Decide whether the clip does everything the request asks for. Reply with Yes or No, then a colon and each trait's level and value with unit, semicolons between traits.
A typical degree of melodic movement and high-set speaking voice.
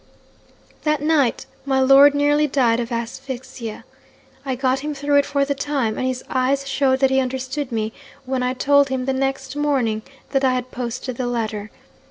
No: narrow, 2.0 semitones; very high, 265 Hz